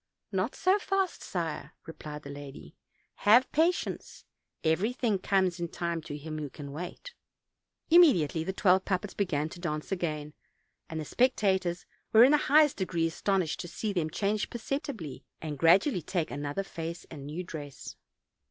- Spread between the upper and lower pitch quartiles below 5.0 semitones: No, wide, 5.5 semitones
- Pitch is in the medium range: Yes, medium, 175 Hz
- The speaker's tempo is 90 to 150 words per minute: No, average, 160 wpm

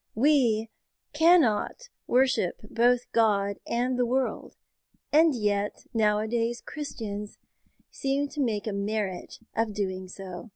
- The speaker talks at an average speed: No, slow, 115 wpm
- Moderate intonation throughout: Yes, average, 3.8 semitones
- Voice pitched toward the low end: No, high, 225 Hz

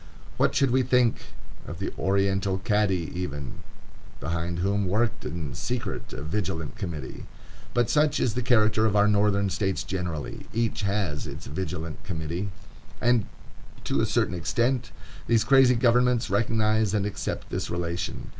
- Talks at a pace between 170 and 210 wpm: No, average, 145 wpm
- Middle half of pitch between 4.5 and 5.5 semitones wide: Yes, average, 4.9 semitones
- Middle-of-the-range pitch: No, low, 100 Hz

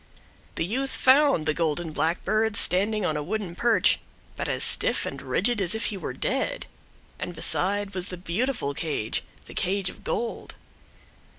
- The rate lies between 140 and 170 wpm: Yes, average, 165 wpm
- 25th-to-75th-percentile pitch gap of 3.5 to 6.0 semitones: Yes, average, 4.8 semitones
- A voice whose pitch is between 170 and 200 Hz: Yes, high, 190 Hz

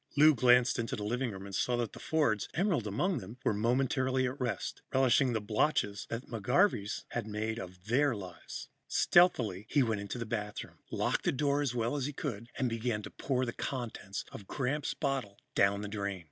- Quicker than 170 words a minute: Yes, average, 200 wpm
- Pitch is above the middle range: No, low, 120 Hz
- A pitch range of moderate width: Yes, average, 4.4 semitones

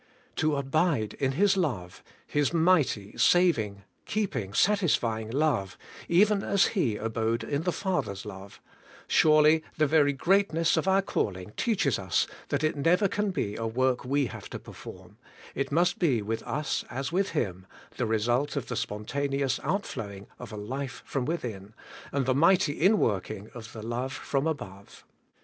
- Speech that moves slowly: No, average, 165 wpm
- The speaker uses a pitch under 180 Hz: Yes, medium, 140 Hz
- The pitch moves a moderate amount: No, wide, 7.0 semitones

